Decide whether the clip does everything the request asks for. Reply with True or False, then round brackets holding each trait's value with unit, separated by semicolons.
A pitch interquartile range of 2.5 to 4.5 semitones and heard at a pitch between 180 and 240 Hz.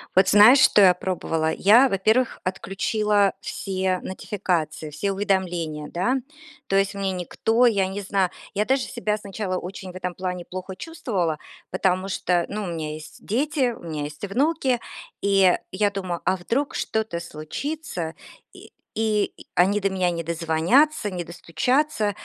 True (3.2 semitones; 190 Hz)